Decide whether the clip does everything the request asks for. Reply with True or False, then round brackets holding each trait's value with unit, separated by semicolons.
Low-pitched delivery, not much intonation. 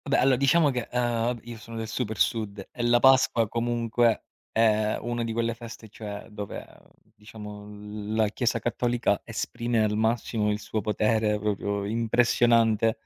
True (115 Hz; 1.9 semitones)